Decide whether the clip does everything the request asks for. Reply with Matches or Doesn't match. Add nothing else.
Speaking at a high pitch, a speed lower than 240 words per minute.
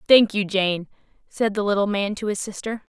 Matches